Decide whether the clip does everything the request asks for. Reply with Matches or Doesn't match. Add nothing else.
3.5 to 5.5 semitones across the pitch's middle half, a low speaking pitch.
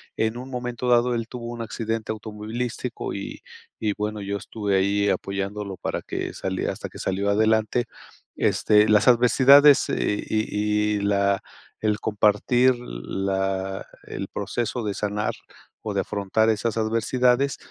Doesn't match